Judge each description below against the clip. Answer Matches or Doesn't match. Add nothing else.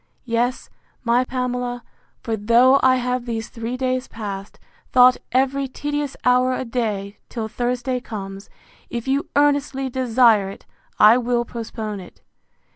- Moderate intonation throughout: Doesn't match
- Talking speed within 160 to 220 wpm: Doesn't match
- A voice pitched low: Doesn't match